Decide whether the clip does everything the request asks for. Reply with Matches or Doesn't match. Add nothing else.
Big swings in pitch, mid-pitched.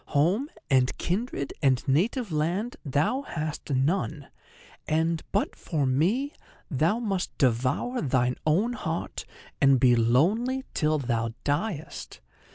Matches